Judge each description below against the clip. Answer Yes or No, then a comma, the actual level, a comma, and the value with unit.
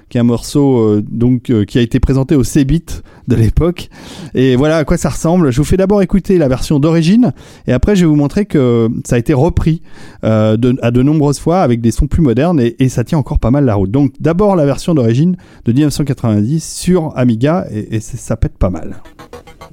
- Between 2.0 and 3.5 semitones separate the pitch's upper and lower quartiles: No, wide, 5.4 semitones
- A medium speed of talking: No, fast, 230 wpm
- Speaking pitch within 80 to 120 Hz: No, medium, 140 Hz